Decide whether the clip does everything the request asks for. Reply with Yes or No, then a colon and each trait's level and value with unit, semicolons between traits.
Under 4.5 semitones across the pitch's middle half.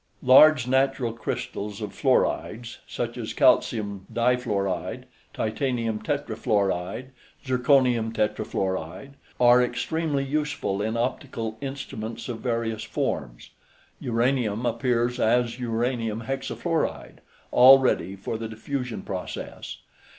Yes: average, 3.0 semitones